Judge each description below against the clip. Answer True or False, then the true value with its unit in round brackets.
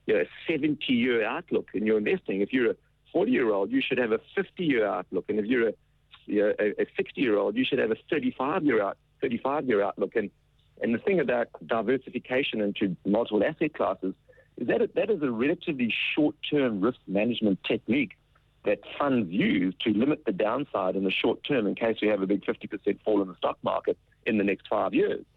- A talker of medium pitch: False (130 Hz)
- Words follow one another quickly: False (190 wpm)